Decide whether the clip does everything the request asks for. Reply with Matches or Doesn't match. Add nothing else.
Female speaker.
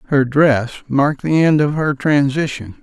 Doesn't match